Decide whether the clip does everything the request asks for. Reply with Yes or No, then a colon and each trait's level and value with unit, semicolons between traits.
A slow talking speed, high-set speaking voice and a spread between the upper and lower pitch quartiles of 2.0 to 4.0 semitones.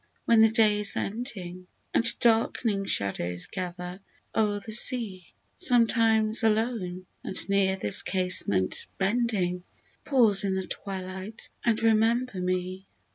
Yes: slow, 120 wpm; high, 205 Hz; average, 3.5 semitones